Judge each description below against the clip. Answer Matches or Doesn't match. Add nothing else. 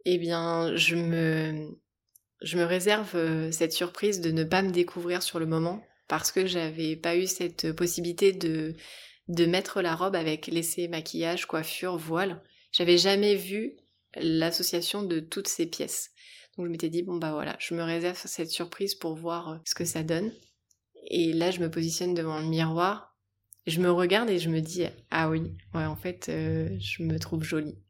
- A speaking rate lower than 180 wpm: Doesn't match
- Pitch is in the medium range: Matches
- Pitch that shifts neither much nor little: Doesn't match